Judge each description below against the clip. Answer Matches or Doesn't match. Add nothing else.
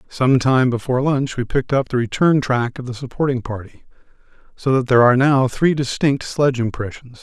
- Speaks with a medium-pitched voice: Doesn't match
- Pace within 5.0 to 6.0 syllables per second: Matches